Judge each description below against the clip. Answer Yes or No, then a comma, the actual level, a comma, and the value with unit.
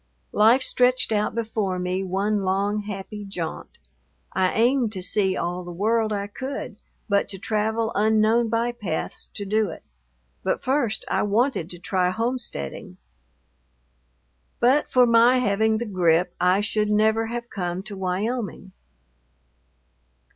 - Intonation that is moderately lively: Yes, average, 3.3 semitones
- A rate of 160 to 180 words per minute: No, slow, 135 wpm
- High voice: Yes, high, 210 Hz